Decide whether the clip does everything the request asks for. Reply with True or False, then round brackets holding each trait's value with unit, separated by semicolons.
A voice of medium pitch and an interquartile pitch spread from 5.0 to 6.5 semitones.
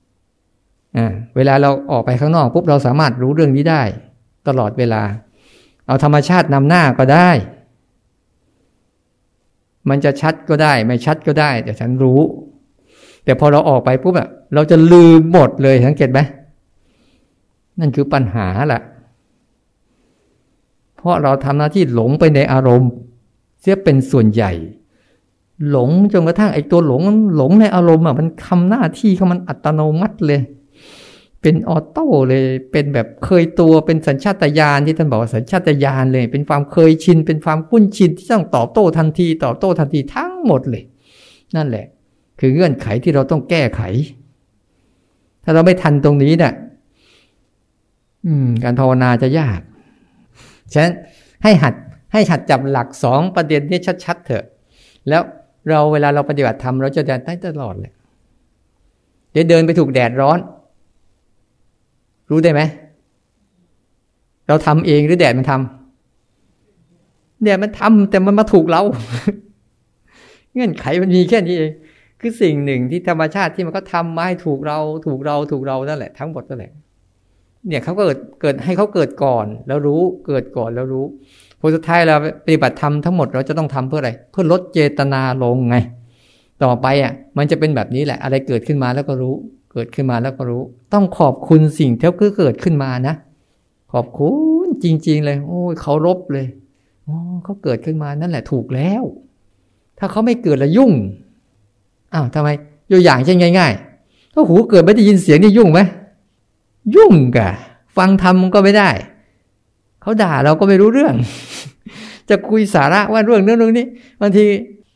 True (145 Hz; 5.3 semitones)